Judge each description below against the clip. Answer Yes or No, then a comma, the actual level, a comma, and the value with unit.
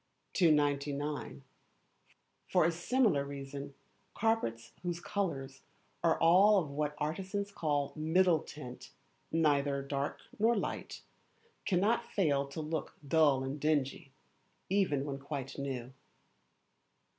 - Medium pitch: Yes, medium, 150 Hz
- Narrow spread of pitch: No, average, 3.9 semitones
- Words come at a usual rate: No, slow, 110 wpm